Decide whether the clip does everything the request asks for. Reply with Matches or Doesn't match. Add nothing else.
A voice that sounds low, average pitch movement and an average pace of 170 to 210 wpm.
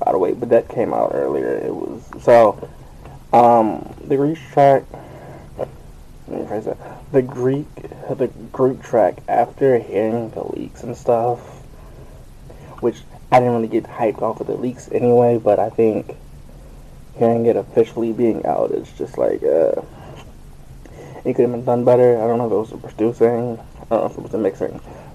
Matches